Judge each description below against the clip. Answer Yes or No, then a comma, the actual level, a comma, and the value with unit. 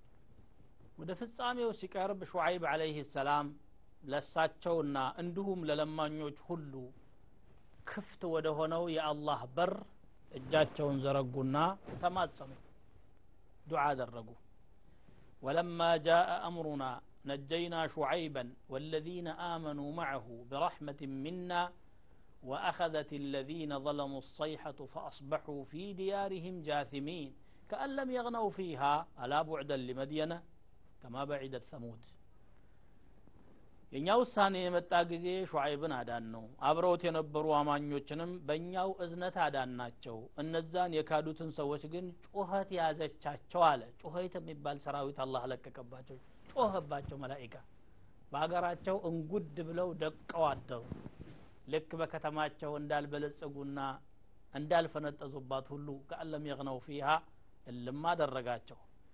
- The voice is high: No, medium, 150 Hz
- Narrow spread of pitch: No, average, 3.9 semitones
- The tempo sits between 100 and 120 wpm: No, average, 90 wpm